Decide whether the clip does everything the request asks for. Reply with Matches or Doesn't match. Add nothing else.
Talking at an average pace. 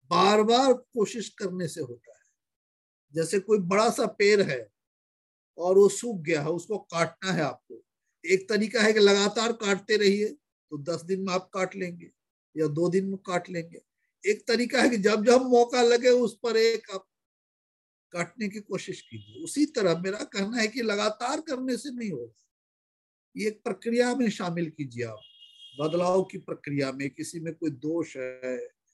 Matches